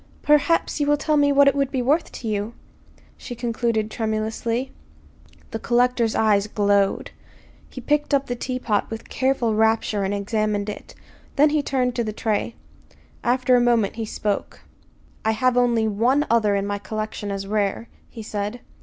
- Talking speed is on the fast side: No, average, 170 wpm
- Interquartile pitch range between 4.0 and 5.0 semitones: No, average, 3.1 semitones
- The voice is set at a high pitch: Yes, high, 230 Hz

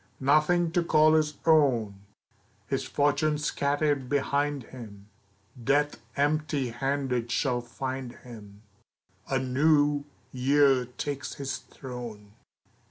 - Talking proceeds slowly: Yes, slow, 100 wpm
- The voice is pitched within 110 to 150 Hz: Yes, medium, 140 Hz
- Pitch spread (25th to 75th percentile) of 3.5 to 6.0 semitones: No, average, 3.0 semitones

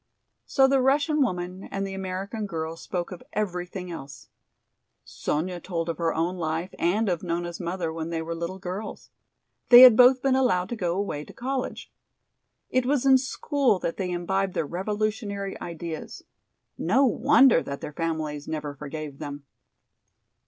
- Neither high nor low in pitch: Yes, medium, 180 Hz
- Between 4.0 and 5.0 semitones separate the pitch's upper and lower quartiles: Yes, average, 4.7 semitones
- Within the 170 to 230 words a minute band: No, average, 160 wpm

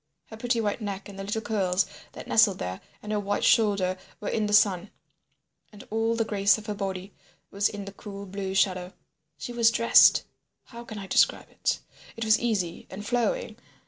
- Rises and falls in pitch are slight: Yes, narrow, 2.2 semitones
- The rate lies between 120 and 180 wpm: No, average, 190 wpm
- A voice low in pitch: No, high, 205 Hz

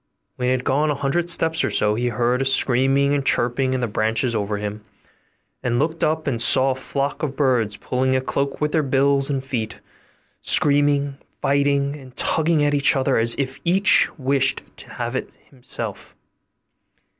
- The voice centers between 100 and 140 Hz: Yes, low, 135 Hz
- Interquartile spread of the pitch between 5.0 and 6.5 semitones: No, narrow, 2.4 semitones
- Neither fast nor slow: Yes, average, 180 wpm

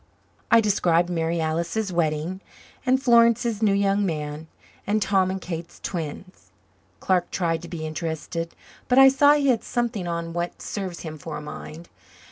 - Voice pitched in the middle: Yes, medium, 175 Hz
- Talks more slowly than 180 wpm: Yes, average, 160 wpm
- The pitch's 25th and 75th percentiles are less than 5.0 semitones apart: Yes, average, 4.4 semitones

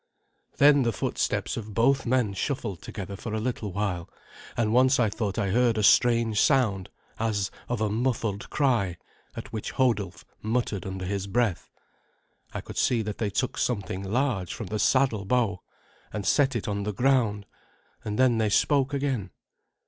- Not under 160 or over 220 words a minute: Yes, average, 170 wpm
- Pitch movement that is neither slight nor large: Yes, average, 3.7 semitones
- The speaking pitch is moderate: No, low, 110 Hz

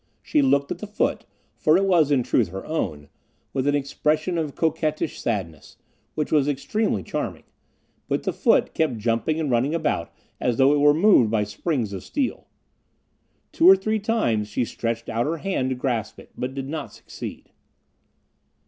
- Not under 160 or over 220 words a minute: Yes, average, 175 wpm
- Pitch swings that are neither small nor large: No, wide, 5.7 semitones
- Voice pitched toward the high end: No, medium, 145 Hz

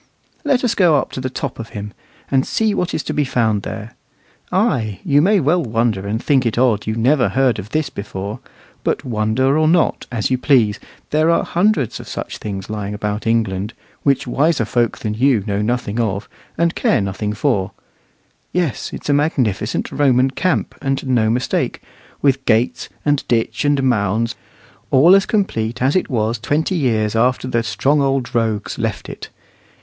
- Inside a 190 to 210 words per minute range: No, average, 180 wpm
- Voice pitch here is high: No, low, 125 Hz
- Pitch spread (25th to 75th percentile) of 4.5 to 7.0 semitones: Yes, average, 5.0 semitones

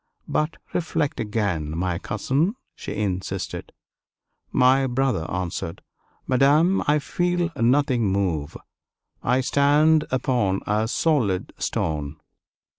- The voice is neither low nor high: No, low, 125 Hz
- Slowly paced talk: Yes, slow, 100 wpm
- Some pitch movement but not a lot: No, wide, 7.7 semitones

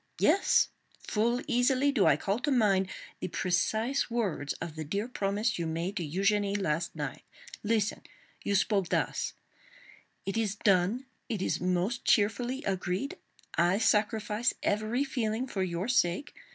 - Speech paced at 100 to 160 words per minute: Yes, average, 140 wpm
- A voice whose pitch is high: Yes, high, 205 Hz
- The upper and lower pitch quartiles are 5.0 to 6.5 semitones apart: No, average, 4.3 semitones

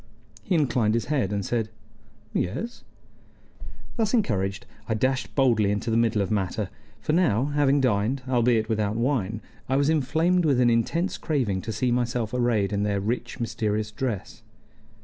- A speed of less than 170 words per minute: Yes, average, 160 wpm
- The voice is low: Yes, low, 115 Hz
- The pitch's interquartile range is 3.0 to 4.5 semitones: Yes, average, 4.2 semitones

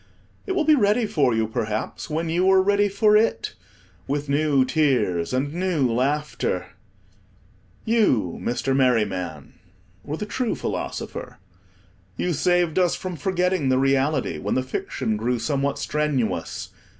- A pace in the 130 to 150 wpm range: Yes, average, 140 wpm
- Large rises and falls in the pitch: Yes, wide, 6.5 semitones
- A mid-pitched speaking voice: Yes, medium, 145 Hz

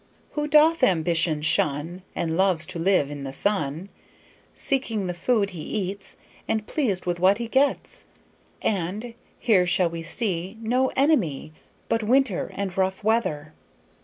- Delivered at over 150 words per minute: No, average, 145 wpm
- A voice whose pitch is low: No, high, 190 Hz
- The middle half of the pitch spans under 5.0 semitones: No, average, 5.3 semitones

